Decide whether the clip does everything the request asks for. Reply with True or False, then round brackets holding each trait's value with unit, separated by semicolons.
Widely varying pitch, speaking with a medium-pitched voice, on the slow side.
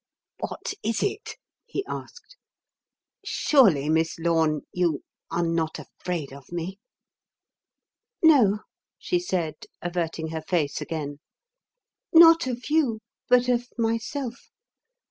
True (7.6 semitones; 180 Hz; 105 wpm)